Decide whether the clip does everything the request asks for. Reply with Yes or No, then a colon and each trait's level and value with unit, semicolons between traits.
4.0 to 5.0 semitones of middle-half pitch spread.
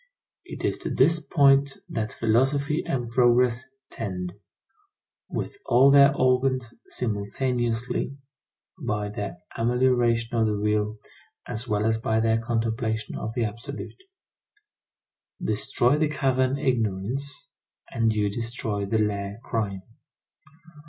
No: average, 3.3 semitones